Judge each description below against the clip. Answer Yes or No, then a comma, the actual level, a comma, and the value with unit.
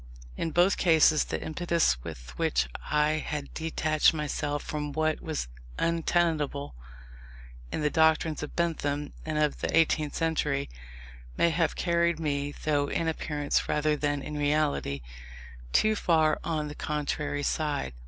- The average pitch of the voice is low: No, medium, 150 Hz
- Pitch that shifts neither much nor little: No, narrow, 1.9 semitones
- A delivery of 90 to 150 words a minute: Yes, average, 140 wpm